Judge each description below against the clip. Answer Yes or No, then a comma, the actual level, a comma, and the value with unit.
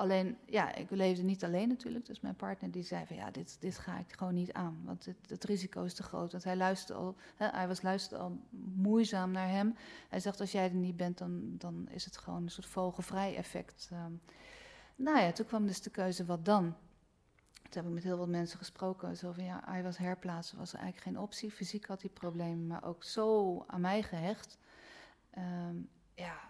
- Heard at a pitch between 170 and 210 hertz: Yes, medium, 185 Hz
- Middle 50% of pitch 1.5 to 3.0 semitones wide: Yes, narrow, 2.4 semitones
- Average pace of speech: No, fast, 215 wpm